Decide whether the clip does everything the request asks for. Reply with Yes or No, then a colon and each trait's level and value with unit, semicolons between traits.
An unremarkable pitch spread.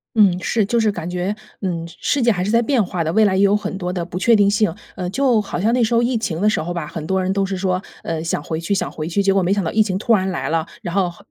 Yes: average, 3.2 semitones